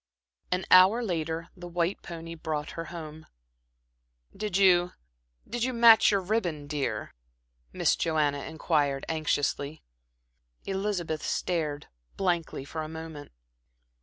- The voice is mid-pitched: Yes, medium, 165 Hz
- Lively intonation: No, average, 3.1 semitones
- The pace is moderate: No, slow, 115 wpm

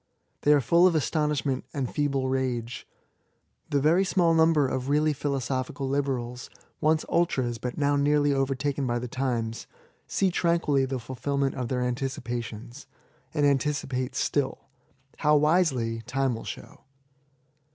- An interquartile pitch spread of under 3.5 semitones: Yes, average, 2.8 semitones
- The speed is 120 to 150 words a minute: Yes, average, 145 wpm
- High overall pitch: No, low, 135 Hz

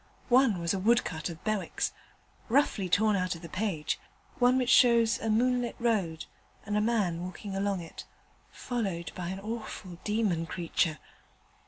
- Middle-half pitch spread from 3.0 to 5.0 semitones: Yes, average, 4.7 semitones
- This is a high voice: Yes, high, 200 Hz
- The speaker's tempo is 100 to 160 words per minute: Yes, average, 155 wpm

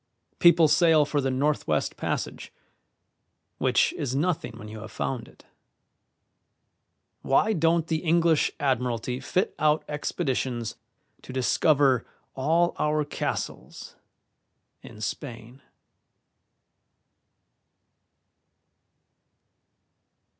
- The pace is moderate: No, slow, 85 wpm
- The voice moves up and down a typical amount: Yes, average, 4.1 semitones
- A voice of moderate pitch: Yes, medium, 145 Hz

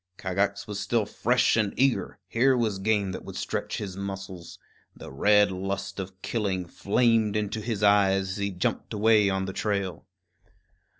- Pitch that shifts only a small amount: Yes, narrow, 2.0 semitones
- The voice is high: No, low, 100 Hz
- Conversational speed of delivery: Yes, average, 165 wpm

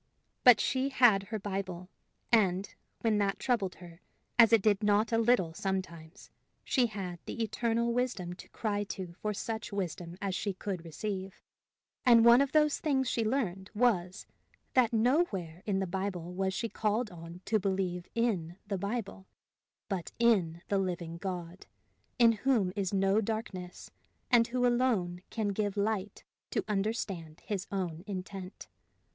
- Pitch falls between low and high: No, high, 200 Hz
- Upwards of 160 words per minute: No, average, 155 wpm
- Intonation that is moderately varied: Yes, average, 3.8 semitones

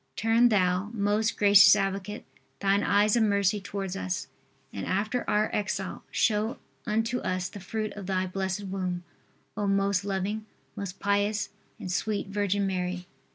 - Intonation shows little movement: Yes, narrow, 1.8 semitones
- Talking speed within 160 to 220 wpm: No, average, 150 wpm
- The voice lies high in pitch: Yes, high, 200 Hz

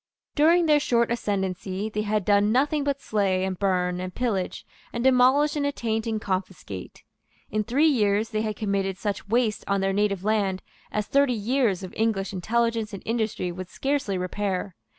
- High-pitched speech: Yes, high, 210 Hz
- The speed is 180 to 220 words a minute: No, average, 170 wpm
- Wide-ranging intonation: No, average, 3.7 semitones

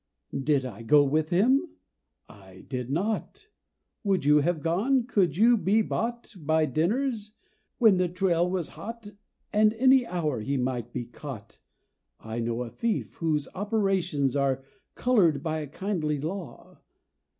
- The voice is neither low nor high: Yes, medium, 170 Hz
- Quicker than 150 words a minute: No, average, 145 wpm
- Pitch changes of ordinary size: No, wide, 7.0 semitones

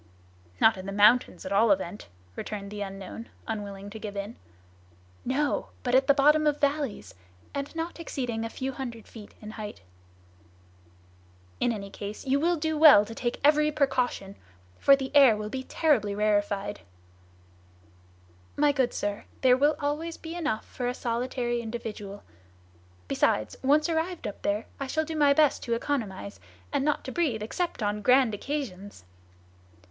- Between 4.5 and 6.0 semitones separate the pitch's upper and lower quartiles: Yes, wide, 5.6 semitones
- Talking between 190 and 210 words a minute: No, average, 165 wpm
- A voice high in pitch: Yes, high, 245 Hz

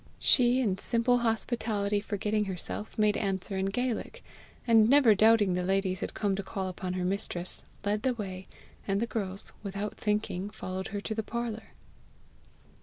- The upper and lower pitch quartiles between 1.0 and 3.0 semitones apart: Yes, average, 2.7 semitones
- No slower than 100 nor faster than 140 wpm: No, average, 165 wpm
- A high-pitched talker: Yes, high, 205 Hz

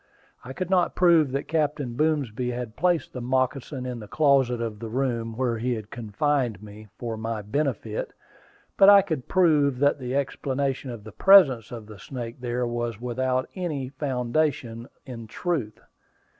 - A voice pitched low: Yes, low, 125 Hz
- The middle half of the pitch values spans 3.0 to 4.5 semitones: Yes, average, 3.8 semitones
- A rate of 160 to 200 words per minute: Yes, average, 165 wpm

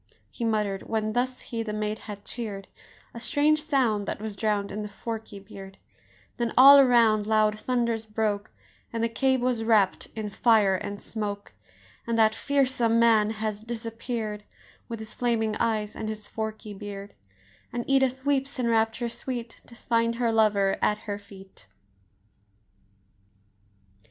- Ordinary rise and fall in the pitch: No, narrow, 2.1 semitones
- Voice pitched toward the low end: No, high, 220 Hz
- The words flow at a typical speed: Yes, average, 150 wpm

